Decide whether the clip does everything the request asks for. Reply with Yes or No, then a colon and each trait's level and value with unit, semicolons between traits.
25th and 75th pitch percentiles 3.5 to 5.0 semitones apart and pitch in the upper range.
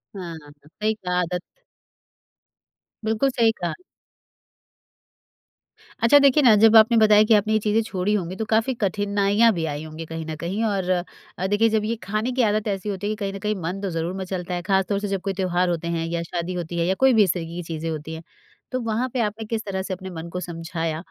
Yes: average, 3.9 semitones; high, 195 Hz